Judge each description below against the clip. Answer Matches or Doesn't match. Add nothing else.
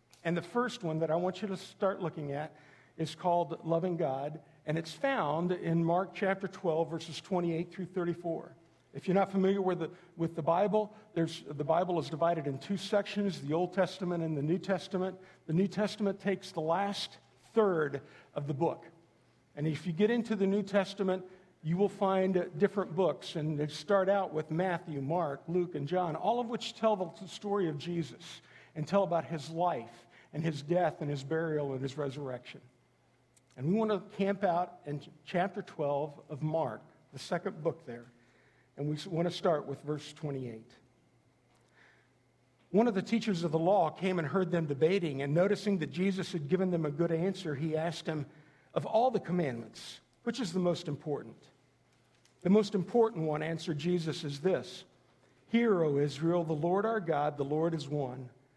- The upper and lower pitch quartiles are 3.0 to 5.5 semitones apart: Matches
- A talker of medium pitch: Matches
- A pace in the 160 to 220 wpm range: Matches